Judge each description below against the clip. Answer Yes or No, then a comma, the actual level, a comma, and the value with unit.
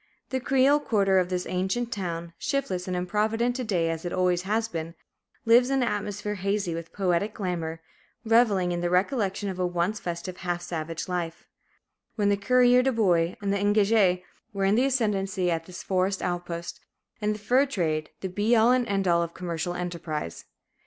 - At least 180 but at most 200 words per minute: Yes, average, 185 wpm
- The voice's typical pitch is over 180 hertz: Yes, high, 190 Hz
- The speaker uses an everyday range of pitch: Yes, average, 3.7 semitones